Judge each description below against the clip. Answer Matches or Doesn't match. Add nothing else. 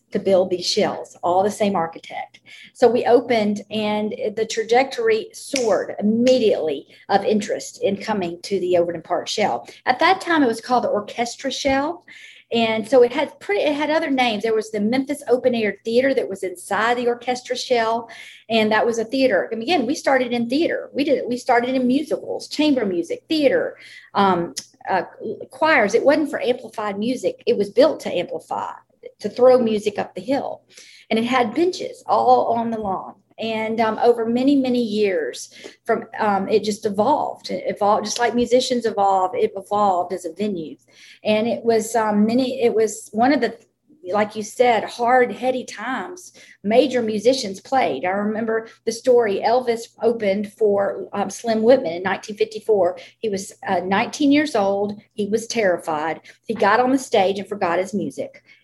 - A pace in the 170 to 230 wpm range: Matches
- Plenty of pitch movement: Doesn't match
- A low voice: Doesn't match